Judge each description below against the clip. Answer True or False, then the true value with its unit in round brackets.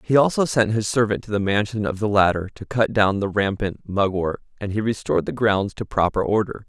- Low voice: True (105 Hz)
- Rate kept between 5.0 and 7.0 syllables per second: True (5.6 syllables/s)